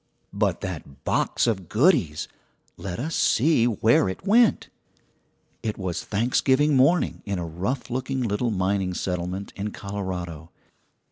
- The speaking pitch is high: No, low, 100 Hz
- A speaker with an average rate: No, slow, 130 wpm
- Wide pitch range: Yes, wide, 5.9 semitones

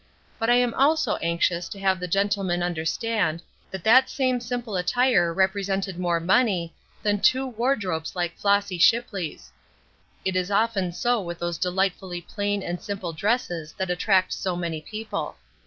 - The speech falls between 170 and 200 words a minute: No, average, 155 wpm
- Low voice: No, high, 190 Hz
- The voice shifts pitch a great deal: No, average, 4.1 semitones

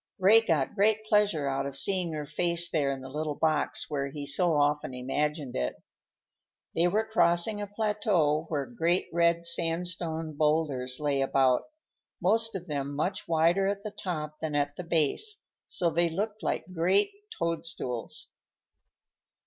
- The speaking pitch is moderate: Yes, medium, 165 Hz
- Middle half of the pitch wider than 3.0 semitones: Yes, average, 4.3 semitones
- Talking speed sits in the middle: Yes, average, 155 wpm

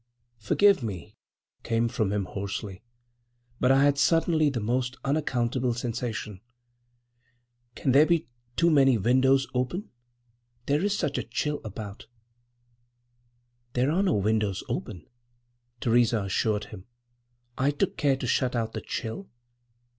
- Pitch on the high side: No, low, 125 Hz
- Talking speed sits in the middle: No, slow, 120 wpm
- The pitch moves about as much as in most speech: Yes, average, 4.6 semitones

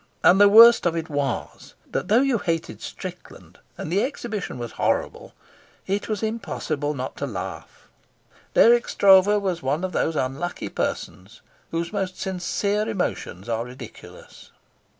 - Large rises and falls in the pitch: Yes, wide, 6.3 semitones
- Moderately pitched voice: Yes, medium, 180 Hz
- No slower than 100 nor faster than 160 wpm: Yes, average, 145 wpm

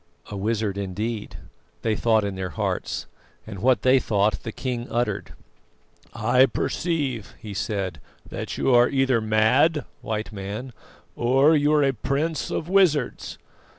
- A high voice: No, low, 120 Hz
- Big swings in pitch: No, average, 4.3 semitones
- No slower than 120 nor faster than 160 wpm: Yes, average, 145 wpm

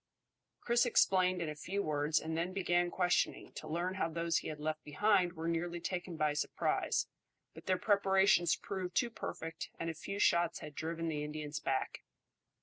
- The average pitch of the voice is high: No, medium, 170 Hz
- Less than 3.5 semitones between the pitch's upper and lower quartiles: Yes, average, 3.0 semitones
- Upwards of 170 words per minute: Yes, average, 180 wpm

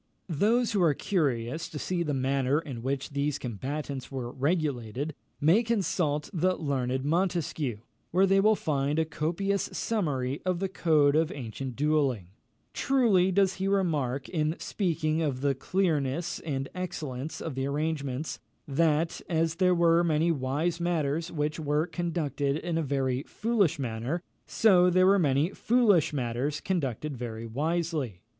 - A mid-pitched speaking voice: Yes, medium, 155 Hz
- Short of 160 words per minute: Yes, average, 150 wpm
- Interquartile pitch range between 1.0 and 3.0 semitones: No, average, 4.3 semitones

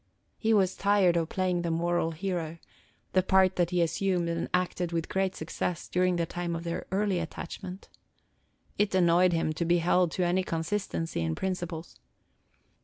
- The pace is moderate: Yes, average, 170 wpm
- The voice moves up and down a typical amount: No, narrow, 1.9 semitones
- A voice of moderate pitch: Yes, medium, 175 Hz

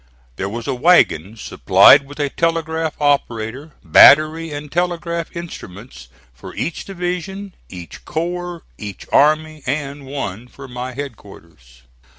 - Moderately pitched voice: Yes, medium, 145 Hz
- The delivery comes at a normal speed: No, slow, 125 wpm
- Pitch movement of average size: No, wide, 6.0 semitones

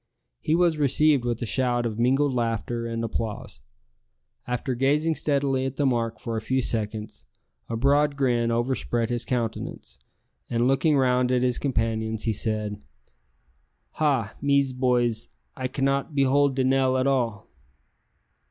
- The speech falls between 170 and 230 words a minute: No, average, 150 wpm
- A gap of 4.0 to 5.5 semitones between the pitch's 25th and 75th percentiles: No, average, 2.9 semitones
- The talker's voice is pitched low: Yes, low, 125 Hz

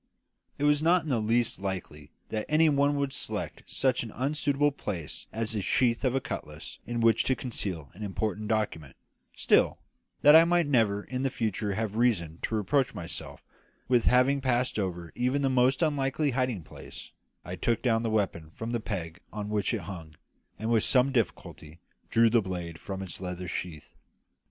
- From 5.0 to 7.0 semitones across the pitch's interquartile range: Yes, wide, 5.5 semitones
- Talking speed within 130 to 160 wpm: No, average, 185 wpm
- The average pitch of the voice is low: Yes, low, 115 Hz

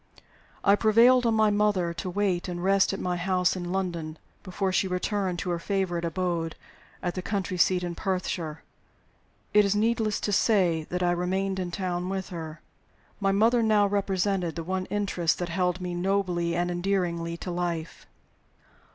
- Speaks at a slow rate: No, average, 170 wpm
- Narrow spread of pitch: Yes, narrow, 2.2 semitones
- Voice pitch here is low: No, medium, 185 Hz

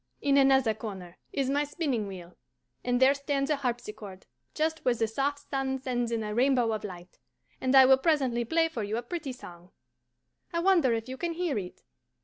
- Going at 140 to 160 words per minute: No, average, 195 wpm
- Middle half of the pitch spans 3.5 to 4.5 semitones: Yes, average, 4.2 semitones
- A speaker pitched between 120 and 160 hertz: No, very high, 260 Hz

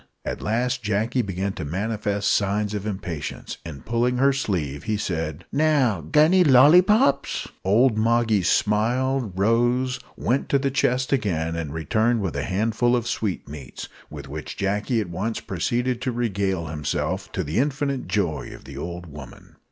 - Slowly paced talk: No, average, 155 wpm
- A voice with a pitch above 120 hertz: No, low, 105 Hz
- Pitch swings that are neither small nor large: No, wide, 6.1 semitones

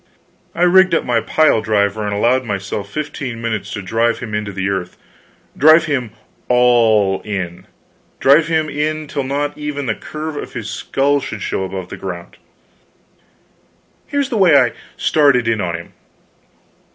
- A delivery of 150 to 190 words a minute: Yes, average, 160 wpm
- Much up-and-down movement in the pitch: Yes, wide, 6.4 semitones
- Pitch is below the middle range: Yes, low, 120 Hz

